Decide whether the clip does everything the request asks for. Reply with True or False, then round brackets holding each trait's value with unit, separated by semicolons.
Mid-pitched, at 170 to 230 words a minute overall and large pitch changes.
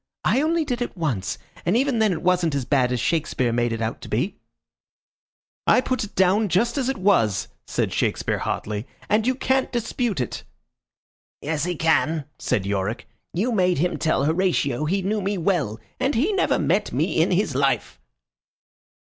True (180 Hz; 180 wpm; 8.4 semitones)